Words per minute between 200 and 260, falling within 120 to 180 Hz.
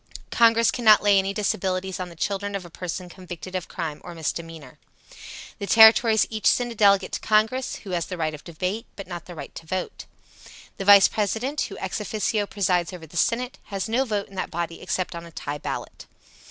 No: fast, 205 wpm; high, 190 Hz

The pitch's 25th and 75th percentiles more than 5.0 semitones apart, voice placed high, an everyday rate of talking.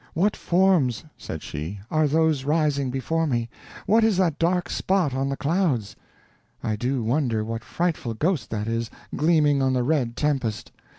No: wide, 5.6 semitones; medium, 140 Hz; average, 165 wpm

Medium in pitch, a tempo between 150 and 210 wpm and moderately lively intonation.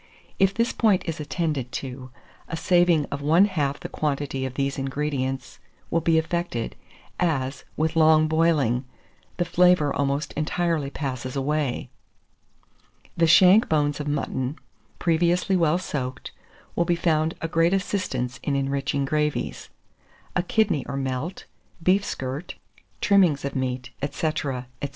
No: medium, 150 Hz; slow, 135 wpm; average, 3.9 semitones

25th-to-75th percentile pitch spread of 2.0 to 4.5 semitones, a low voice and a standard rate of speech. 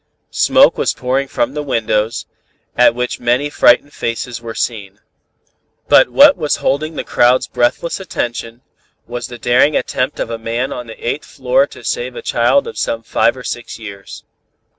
Yes: average, 4.1 semitones; low, 125 Hz; average, 170 wpm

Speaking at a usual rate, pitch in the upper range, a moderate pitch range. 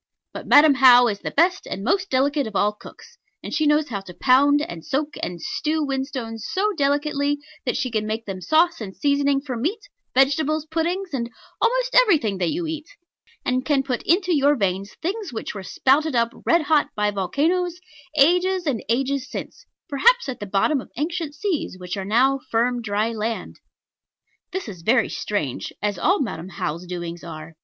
No: average, 185 wpm; very high, 275 Hz; wide, 6.6 semitones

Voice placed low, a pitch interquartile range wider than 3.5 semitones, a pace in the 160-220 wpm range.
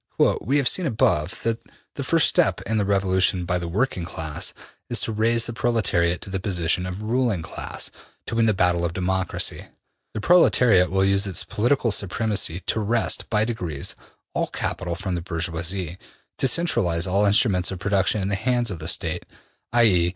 Yes: very low, 95 Hz; average, 4.1 semitones; average, 180 wpm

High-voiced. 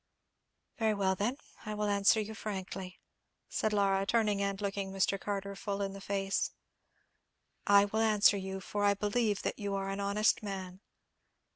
Yes: high, 200 Hz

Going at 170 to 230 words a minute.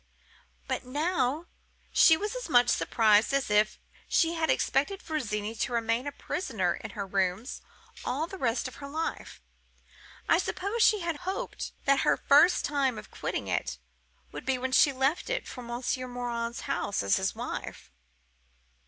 No: average, 160 wpm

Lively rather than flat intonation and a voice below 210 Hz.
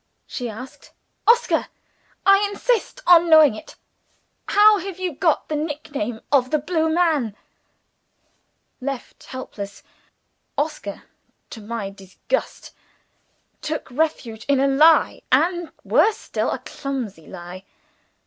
No: wide, 6.5 semitones; very high, 290 Hz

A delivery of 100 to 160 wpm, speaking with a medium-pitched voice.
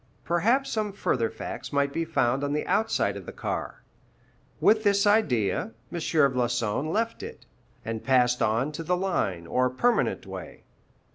Yes: average, 155 wpm; medium, 145 Hz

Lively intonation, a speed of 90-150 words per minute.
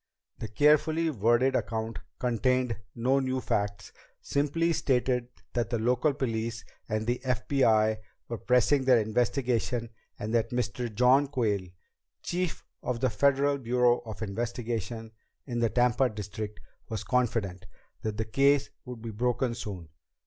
No: average, 2.9 semitones; slow, 135 wpm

